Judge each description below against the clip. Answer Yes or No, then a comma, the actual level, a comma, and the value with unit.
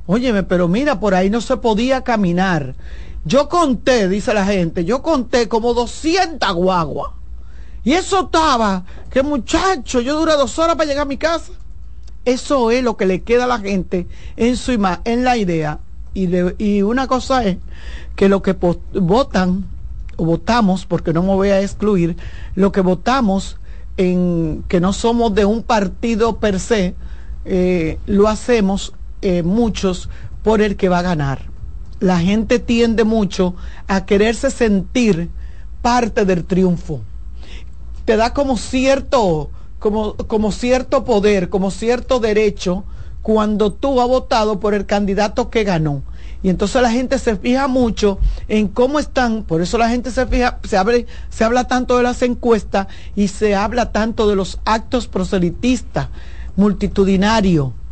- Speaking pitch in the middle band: No, high, 215 Hz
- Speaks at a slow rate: No, average, 160 wpm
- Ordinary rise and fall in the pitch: Yes, average, 4.7 semitones